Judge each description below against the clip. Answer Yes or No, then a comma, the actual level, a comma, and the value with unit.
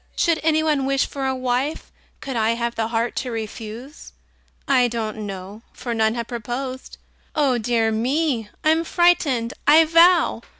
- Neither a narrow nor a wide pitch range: Yes, average, 4.6 semitones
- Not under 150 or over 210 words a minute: Yes, average, 160 wpm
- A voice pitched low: No, very high, 250 Hz